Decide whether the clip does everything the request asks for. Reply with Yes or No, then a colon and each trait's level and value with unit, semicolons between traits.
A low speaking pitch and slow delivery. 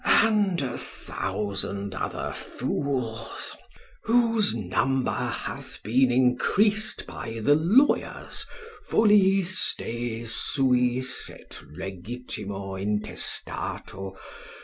Yes: low, 125 Hz; slow, 80 wpm